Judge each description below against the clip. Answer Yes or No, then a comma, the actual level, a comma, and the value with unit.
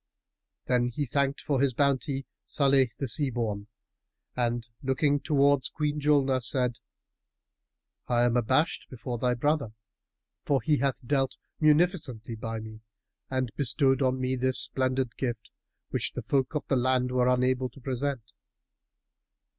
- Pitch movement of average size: No, narrow, 2.3 semitones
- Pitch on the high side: No, low, 130 Hz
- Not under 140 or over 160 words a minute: Yes, average, 145 wpm